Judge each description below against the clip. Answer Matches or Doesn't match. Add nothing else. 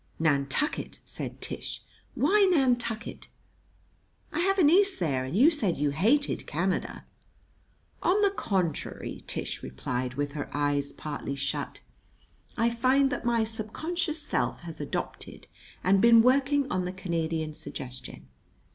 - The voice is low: Doesn't match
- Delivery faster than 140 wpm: Doesn't match